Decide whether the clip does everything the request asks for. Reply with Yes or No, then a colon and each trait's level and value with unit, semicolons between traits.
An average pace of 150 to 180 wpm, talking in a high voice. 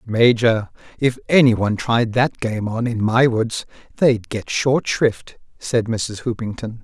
No: average, 160 wpm; low, 115 Hz